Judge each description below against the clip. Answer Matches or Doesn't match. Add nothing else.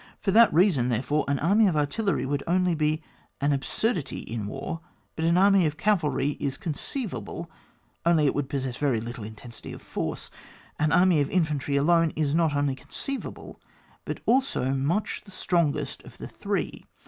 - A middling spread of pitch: Matches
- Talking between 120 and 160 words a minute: Doesn't match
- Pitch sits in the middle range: Matches